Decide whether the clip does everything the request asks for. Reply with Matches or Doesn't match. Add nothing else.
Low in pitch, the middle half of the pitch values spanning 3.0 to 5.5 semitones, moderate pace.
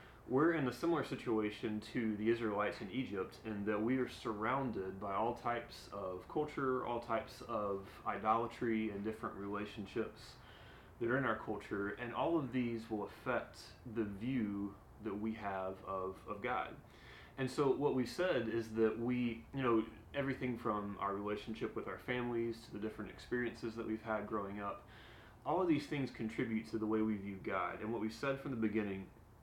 Doesn't match